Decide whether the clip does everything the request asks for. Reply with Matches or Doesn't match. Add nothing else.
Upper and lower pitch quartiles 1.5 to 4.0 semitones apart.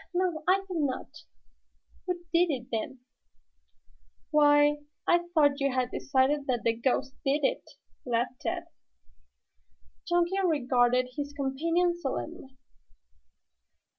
Doesn't match